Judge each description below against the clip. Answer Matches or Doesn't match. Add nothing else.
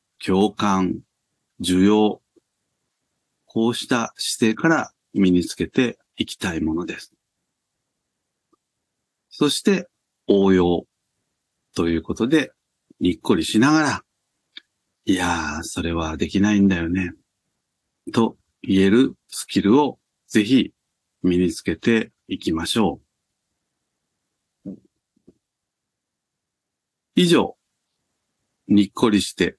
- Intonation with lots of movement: Doesn't match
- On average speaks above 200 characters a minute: Doesn't match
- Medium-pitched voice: Doesn't match